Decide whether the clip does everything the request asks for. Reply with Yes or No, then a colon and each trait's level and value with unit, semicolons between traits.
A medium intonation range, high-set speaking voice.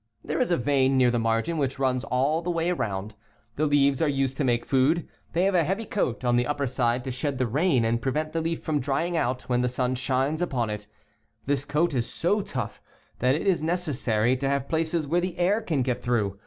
No: average, 4.7 semitones; low, 135 Hz